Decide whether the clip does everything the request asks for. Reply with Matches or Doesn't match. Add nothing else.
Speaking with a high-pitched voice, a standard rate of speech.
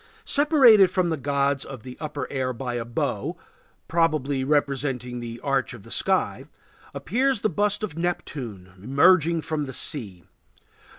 Doesn't match